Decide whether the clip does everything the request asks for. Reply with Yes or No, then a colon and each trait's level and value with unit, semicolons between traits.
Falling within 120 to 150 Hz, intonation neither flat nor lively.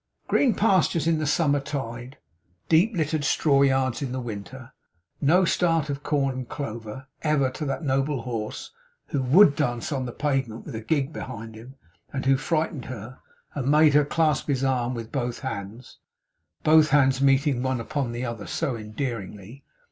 Yes: low, 135 Hz; average, 3.6 semitones